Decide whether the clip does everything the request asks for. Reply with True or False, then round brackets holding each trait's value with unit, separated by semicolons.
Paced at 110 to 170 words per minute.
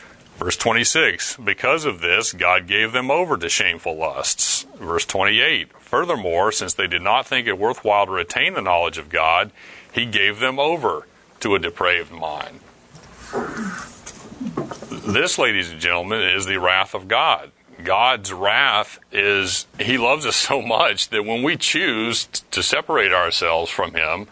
True (155 wpm)